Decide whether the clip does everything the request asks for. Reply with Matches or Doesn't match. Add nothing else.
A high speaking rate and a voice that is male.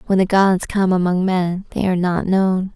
Doesn't match